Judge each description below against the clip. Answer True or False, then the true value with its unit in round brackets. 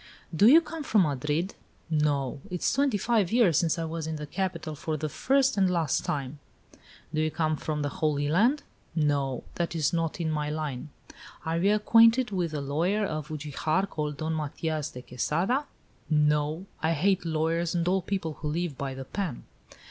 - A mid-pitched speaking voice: True (160 Hz)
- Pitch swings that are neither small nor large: True (4.0 semitones)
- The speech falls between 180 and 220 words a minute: True (185 wpm)